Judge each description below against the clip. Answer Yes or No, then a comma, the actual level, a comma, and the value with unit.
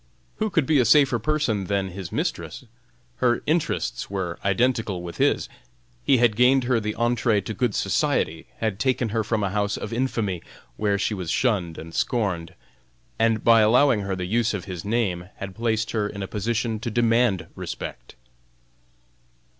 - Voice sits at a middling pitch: No, low, 110 Hz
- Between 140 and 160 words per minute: No, average, 170 wpm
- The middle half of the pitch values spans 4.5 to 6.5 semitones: No, average, 3.6 semitones